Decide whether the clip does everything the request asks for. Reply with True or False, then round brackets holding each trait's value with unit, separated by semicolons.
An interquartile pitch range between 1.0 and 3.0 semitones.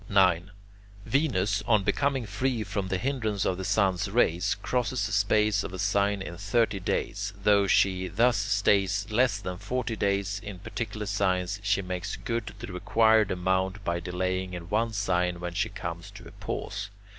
True (2.6 semitones)